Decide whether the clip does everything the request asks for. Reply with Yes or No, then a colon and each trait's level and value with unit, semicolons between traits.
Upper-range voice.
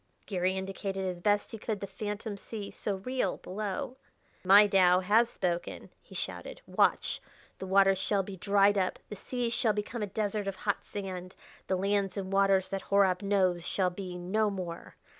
Yes: high, 195 Hz